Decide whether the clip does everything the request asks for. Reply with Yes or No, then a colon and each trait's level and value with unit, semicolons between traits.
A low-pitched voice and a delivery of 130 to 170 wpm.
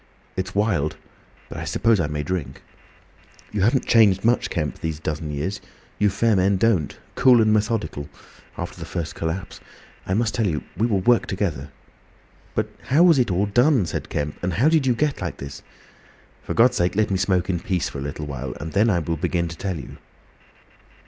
No: very low, 95 Hz; average, 195 wpm